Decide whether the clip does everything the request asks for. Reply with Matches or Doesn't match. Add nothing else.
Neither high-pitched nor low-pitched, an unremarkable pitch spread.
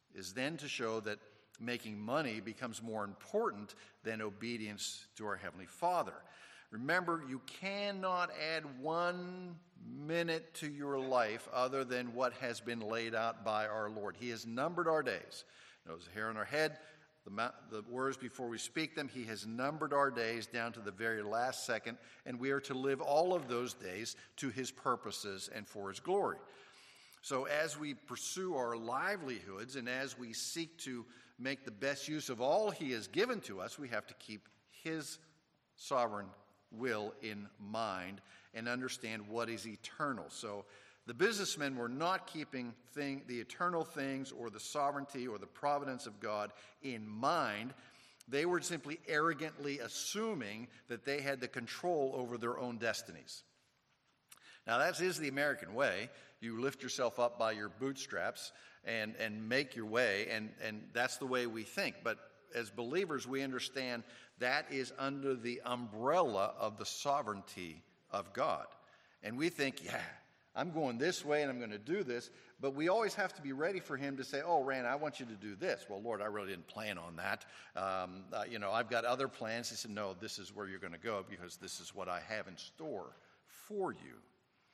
Doesn't match